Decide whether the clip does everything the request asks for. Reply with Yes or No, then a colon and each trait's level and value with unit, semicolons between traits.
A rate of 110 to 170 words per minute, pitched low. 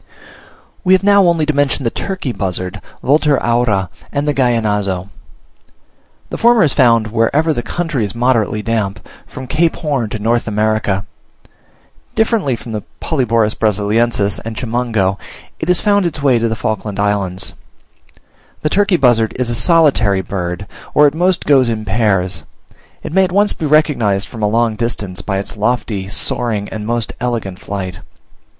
Yes: average, 160 wpm; low, 115 Hz